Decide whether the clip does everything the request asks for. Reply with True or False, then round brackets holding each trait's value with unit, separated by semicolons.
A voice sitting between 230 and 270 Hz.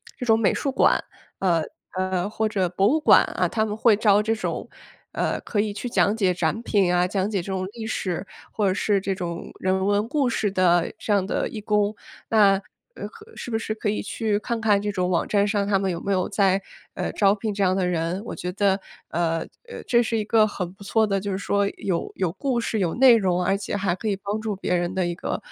False (200 Hz)